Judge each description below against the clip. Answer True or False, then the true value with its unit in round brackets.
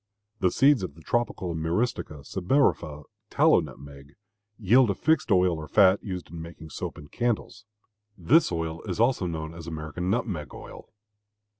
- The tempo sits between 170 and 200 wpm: False (155 wpm)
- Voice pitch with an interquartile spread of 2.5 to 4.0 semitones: False (5.6 semitones)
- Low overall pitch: True (90 Hz)